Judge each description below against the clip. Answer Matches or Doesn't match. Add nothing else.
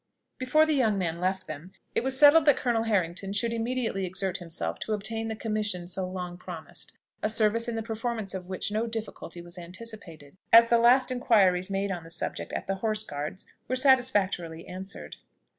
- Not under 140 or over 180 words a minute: Doesn't match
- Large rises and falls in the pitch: Doesn't match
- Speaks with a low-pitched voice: Doesn't match